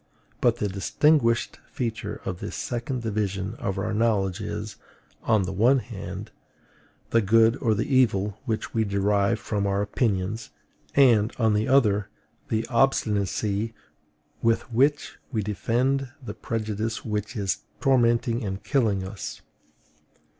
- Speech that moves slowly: Yes, slow, 130 wpm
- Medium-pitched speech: No, low, 110 Hz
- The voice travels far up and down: No, average, 2.7 semitones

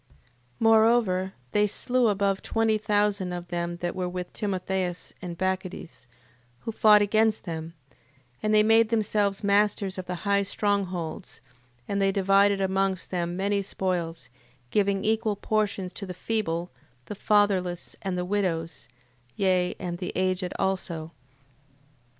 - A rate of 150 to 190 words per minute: No, average, 140 wpm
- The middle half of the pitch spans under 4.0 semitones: Yes, narrow, 2.5 semitones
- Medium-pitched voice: No, high, 195 Hz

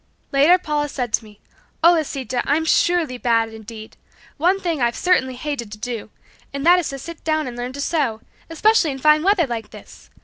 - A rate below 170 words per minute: No, average, 200 wpm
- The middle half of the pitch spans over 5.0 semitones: Yes, wide, 5.4 semitones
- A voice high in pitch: Yes, very high, 280 Hz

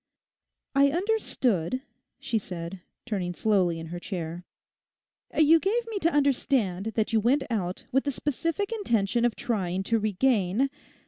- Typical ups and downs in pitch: No, wide, 7.2 semitones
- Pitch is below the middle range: No, high, 225 Hz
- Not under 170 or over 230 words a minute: No, average, 140 wpm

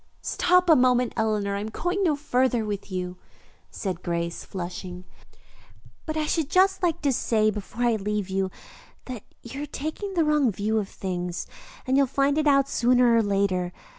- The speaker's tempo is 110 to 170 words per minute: No, average, 180 wpm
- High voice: Yes, high, 235 Hz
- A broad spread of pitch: Yes, wide, 6.5 semitones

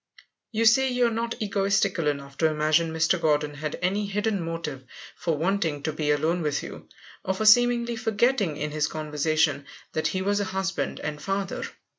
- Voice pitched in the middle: Yes, medium, 170 Hz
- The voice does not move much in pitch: No, average, 5.2 semitones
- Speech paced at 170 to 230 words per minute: Yes, average, 180 wpm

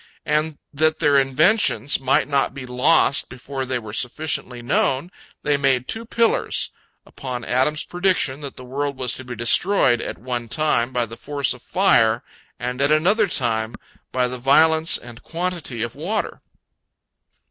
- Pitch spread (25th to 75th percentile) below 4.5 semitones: Yes, average, 3.9 semitones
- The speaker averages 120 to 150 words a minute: No, average, 160 wpm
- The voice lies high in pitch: No, low, 135 Hz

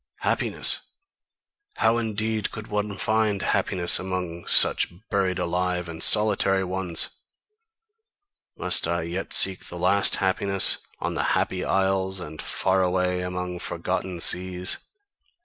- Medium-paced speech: No, slow, 120 wpm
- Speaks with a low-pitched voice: Yes, very low, 95 Hz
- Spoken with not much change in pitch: Yes, narrow, 1.6 semitones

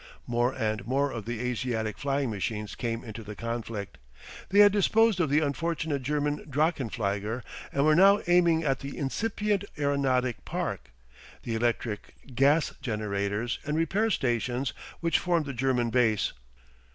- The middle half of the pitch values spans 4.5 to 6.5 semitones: Yes, average, 5.2 semitones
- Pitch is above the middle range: No, low, 130 Hz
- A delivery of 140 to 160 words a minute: Yes, average, 145 wpm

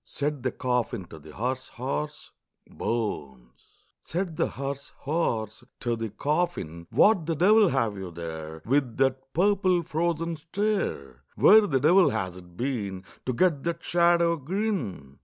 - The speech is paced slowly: No, average, 145 wpm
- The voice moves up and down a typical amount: No, wide, 8.8 semitones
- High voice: No, low, 135 Hz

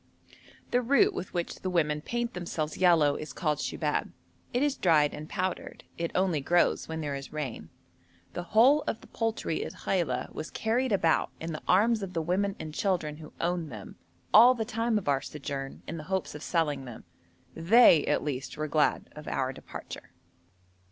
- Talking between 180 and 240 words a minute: Yes, average, 185 wpm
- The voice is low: No, medium, 170 Hz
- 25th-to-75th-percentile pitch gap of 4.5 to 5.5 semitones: Yes, average, 5.2 semitones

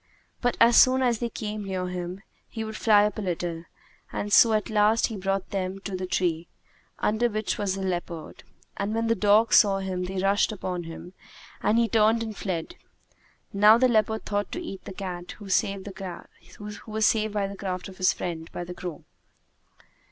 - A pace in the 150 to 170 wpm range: No, average, 190 wpm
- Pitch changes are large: No, average, 2.9 semitones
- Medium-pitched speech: No, high, 200 Hz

